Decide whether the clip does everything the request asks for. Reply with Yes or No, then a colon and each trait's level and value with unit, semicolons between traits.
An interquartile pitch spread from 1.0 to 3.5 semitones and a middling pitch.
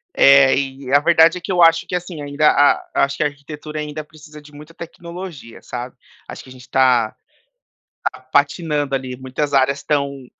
Yes: narrow, 2.6 semitones; medium, 145 Hz